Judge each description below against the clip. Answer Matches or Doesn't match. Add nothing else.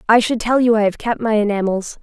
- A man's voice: Doesn't match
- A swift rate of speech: Matches